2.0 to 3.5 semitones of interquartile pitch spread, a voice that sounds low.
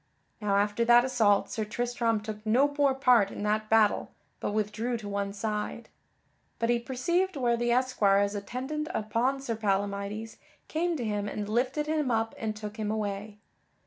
No: average, 3.2 semitones; high, 225 Hz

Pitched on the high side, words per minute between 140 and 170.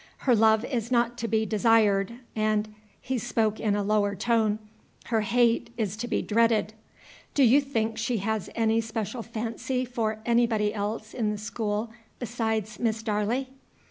Yes: high, 220 Hz; average, 165 wpm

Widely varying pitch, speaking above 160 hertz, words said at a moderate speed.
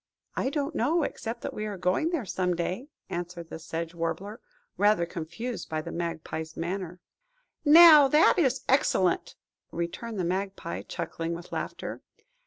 Yes: wide, 6.9 semitones; medium, 185 Hz; average, 150 wpm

